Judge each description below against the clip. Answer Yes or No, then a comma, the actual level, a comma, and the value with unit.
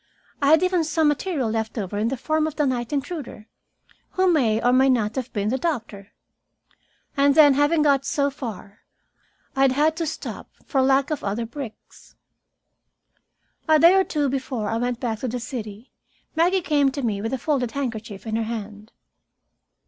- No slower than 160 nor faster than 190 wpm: Yes, average, 185 wpm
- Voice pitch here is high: Yes, very high, 265 Hz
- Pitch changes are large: No, average, 4.8 semitones